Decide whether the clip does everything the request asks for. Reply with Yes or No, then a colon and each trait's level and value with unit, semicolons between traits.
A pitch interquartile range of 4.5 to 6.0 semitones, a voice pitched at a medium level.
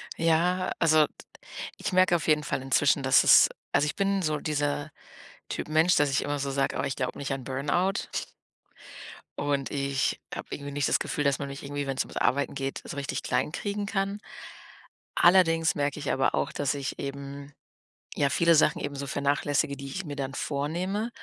No: average, 2.9 semitones; medium, 145 Hz